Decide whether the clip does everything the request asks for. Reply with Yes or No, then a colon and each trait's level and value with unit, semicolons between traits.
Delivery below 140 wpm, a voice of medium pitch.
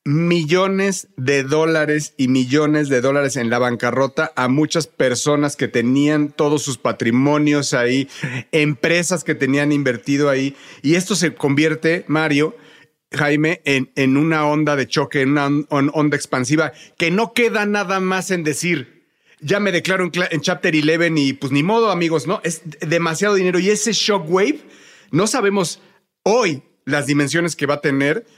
No: average, 160 wpm; medium, 150 Hz